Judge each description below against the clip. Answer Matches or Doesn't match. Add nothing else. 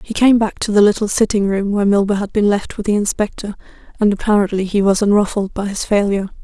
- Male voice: Doesn't match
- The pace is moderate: Doesn't match